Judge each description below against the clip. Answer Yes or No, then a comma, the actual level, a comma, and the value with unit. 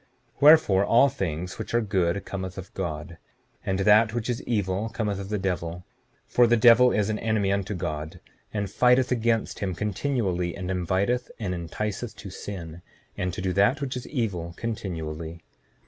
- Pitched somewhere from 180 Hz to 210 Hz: No, low, 100 Hz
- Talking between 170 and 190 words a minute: Yes, average, 175 wpm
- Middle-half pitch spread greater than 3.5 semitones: Yes, average, 4.2 semitones